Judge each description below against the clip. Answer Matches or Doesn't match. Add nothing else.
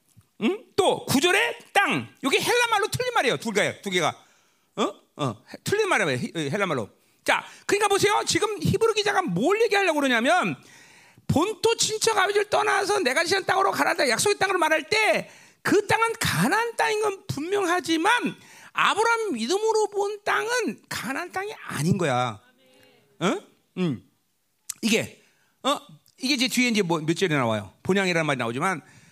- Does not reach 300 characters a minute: Doesn't match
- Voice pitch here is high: Matches